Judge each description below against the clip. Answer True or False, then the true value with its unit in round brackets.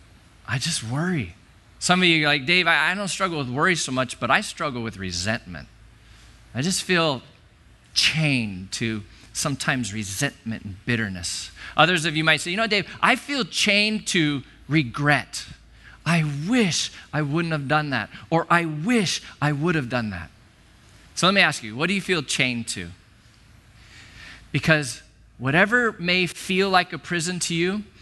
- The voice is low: False (145 Hz)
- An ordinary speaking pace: True (165 wpm)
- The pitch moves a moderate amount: False (7.7 semitones)